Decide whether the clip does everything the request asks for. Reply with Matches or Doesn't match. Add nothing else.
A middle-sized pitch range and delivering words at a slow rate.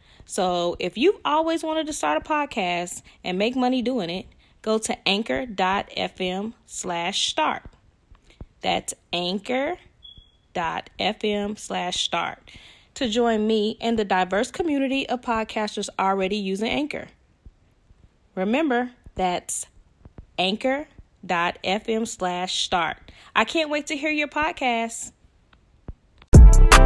Doesn't match